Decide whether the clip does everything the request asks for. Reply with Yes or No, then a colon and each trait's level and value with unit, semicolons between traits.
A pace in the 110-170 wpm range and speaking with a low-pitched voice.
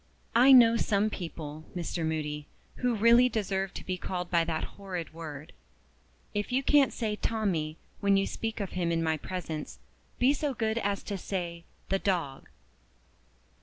No: average, 165 wpm; high, 190 Hz